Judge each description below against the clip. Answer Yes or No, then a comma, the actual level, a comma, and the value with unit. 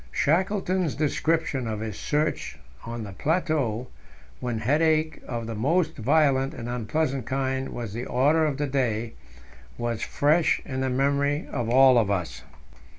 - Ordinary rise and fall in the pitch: Yes, average, 4.7 semitones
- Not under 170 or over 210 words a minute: No, average, 150 wpm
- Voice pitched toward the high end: No, low, 135 Hz